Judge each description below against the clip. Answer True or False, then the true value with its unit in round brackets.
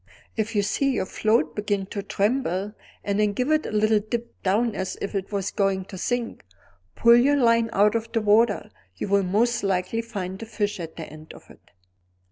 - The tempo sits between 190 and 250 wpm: True (200 wpm)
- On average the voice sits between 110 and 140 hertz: False (210 Hz)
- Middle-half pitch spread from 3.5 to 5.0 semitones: False (2.8 semitones)